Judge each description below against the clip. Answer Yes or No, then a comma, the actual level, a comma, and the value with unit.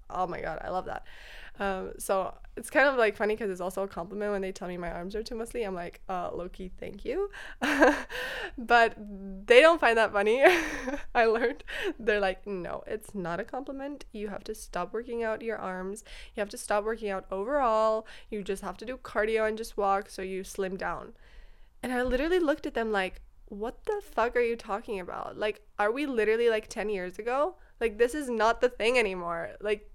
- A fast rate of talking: Yes, fast, 210 wpm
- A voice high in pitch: Yes, high, 220 Hz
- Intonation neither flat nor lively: Yes, average, 3.6 semitones